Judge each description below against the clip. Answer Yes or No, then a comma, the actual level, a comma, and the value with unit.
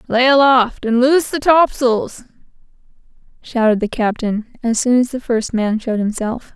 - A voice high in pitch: Yes, high, 240 Hz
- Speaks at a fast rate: No, average, 155 wpm